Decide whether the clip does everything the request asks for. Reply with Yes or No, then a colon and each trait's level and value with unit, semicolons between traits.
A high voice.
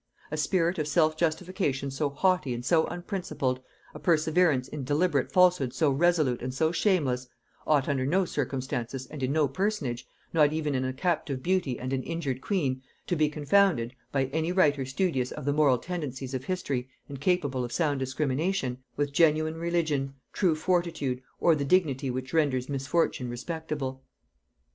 No: medium, 145 Hz